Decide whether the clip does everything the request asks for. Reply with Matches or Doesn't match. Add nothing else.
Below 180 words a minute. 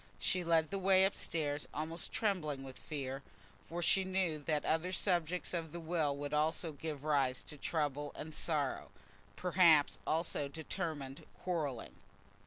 Matches